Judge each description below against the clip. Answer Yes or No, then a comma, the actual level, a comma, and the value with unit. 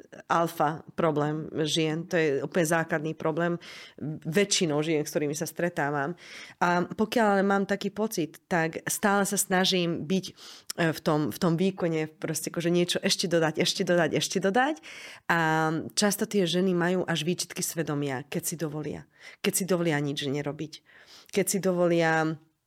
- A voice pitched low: No, medium, 170 Hz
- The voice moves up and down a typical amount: Yes, average, 3.0 semitones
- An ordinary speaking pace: Yes, average, 155 wpm